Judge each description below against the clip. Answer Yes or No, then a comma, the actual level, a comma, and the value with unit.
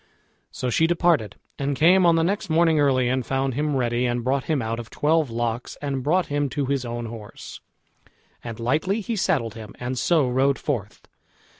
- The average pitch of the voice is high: No, low, 135 Hz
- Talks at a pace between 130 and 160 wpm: No, average, 190 wpm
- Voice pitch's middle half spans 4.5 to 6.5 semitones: Yes, average, 4.8 semitones